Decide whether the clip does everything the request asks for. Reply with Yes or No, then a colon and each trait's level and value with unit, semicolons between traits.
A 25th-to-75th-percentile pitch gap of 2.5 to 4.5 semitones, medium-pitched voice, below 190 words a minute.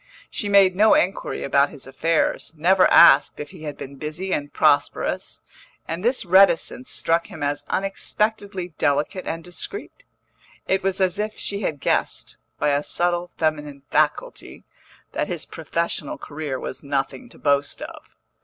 No: average, 4.9 semitones; medium, 165 Hz; average, 155 wpm